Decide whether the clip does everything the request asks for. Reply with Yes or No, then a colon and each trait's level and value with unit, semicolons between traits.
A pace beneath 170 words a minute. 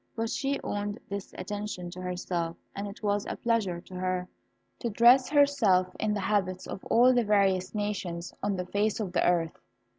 No: average, 185 wpm